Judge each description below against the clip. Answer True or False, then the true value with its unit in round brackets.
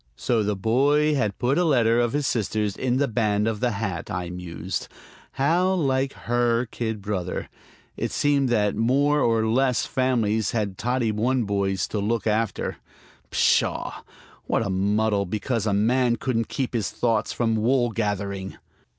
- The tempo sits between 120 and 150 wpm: False (160 wpm)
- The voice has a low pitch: True (115 Hz)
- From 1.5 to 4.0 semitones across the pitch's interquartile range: True (3.7 semitones)